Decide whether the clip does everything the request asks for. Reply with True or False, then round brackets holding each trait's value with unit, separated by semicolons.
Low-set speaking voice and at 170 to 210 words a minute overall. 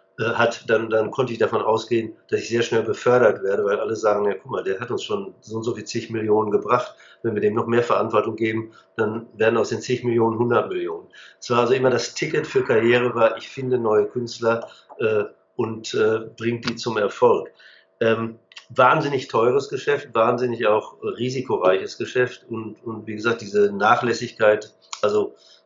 True (120 Hz; 185 wpm)